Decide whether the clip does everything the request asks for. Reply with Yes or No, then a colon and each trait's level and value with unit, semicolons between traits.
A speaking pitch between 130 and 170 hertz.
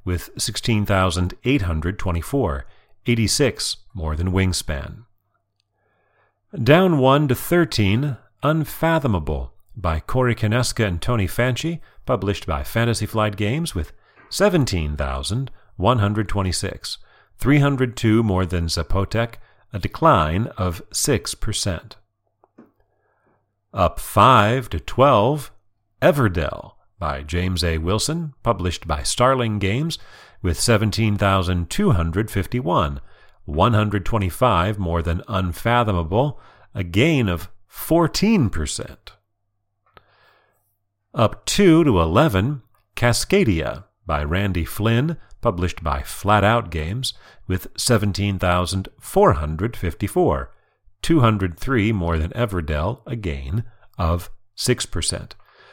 No: low, 105 Hz